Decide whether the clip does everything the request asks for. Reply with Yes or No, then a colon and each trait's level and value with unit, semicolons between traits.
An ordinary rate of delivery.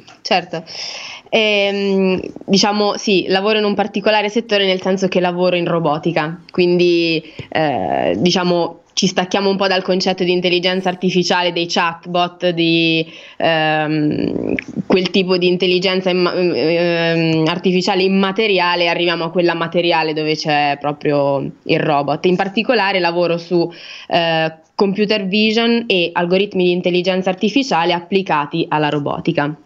Yes: average, 130 wpm